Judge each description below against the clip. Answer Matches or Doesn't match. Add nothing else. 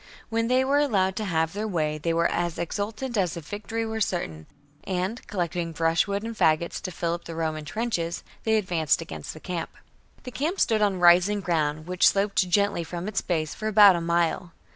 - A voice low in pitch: Doesn't match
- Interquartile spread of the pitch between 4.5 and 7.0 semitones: Doesn't match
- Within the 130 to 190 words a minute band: Doesn't match